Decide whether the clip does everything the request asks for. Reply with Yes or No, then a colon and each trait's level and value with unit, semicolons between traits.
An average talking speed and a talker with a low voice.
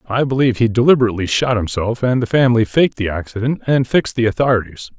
Yes: average, 195 wpm; low, 115 Hz